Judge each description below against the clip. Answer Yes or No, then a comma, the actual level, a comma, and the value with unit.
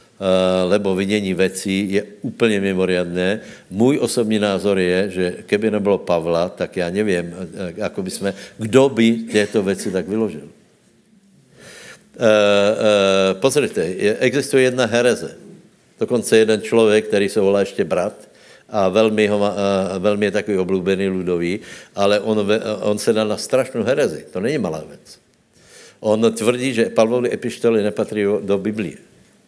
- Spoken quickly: No, average, 125 wpm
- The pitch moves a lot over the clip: No, narrow, 2.5 semitones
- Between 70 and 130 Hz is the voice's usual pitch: Yes, low, 105 Hz